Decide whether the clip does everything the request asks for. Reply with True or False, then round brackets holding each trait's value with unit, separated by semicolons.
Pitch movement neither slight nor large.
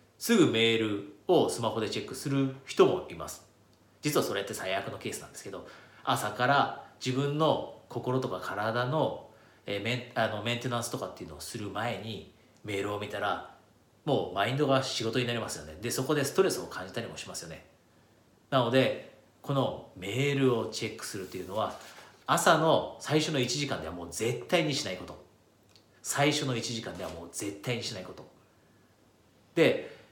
True (4.5 semitones)